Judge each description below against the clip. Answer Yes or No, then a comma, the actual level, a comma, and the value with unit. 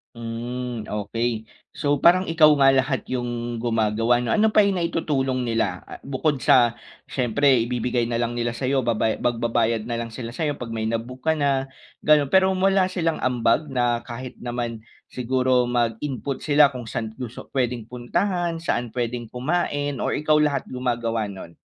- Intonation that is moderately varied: Yes, average, 3.4 semitones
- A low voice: Yes, low, 125 Hz